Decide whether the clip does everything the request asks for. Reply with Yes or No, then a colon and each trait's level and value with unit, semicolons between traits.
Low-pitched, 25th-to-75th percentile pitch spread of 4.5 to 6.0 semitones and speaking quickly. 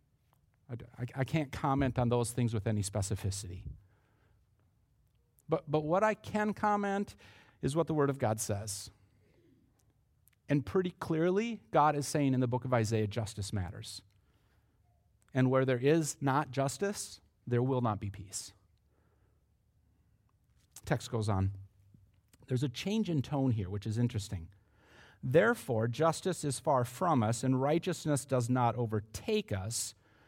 No: low, 120 Hz; average, 5.3 semitones; average, 140 wpm